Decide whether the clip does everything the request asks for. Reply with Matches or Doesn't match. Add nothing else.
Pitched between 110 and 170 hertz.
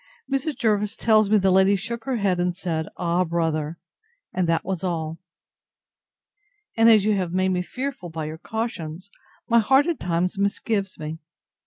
Doesn't match